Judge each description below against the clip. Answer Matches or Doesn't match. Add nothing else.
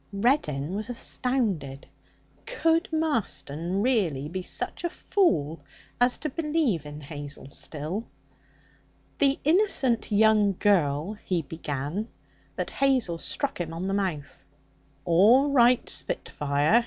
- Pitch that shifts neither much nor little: Doesn't match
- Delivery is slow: Matches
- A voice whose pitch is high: Matches